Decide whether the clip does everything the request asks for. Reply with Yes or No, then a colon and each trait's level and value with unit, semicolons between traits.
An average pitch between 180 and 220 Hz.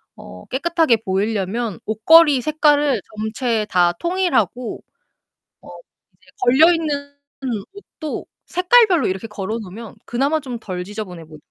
No: high, 240 Hz